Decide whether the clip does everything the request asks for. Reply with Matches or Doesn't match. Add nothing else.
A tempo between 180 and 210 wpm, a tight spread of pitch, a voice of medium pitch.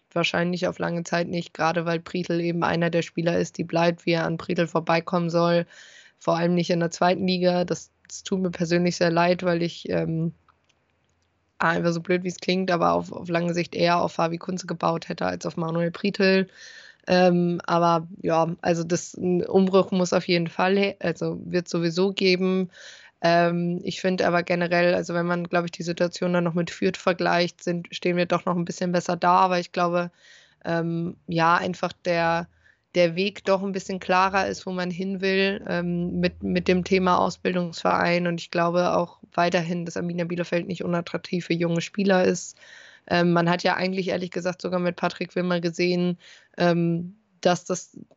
Matches